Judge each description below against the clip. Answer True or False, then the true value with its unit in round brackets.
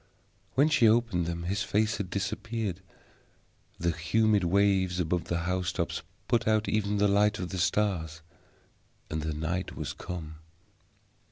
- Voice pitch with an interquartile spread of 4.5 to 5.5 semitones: False (3.5 semitones)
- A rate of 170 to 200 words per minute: False (145 wpm)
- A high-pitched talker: False (95 Hz)